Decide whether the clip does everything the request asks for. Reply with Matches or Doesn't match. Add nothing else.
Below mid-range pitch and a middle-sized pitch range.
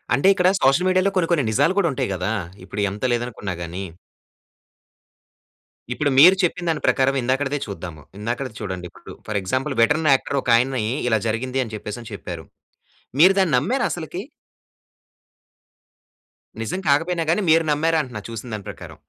Doesn't match